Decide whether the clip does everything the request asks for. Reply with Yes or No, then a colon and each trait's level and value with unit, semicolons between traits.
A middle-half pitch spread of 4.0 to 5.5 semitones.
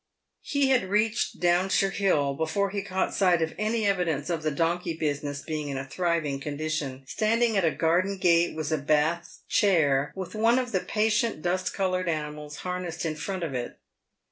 Yes: average, 4.3 semitones